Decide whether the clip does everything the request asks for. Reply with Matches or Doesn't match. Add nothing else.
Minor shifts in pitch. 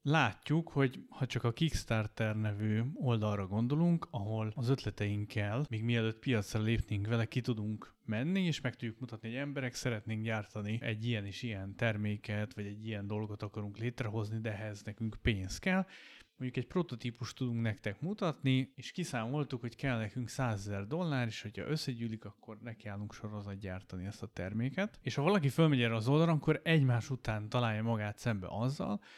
Doesn't match